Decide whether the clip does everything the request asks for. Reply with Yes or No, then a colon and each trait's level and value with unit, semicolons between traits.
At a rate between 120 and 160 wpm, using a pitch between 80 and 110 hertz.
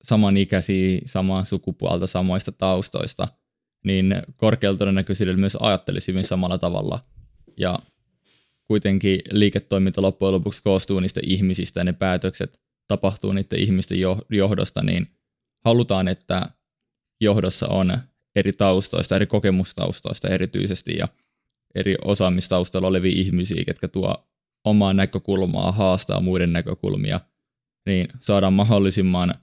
No: average, 110 wpm; very low, 95 Hz